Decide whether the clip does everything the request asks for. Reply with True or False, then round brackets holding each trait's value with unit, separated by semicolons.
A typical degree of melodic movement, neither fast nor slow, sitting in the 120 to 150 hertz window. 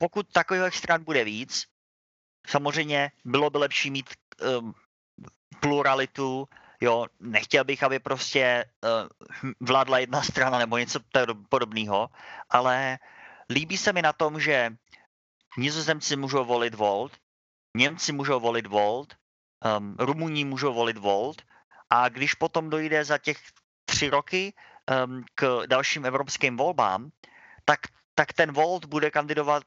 True (3.7 semitones; 125 wpm; 135 Hz)